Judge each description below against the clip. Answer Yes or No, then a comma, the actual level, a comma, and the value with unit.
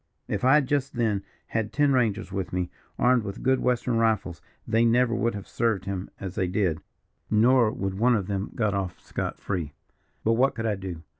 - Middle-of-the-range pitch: No, low, 110 Hz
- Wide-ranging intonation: No, average, 4.1 semitones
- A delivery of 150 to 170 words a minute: No, fast, 205 wpm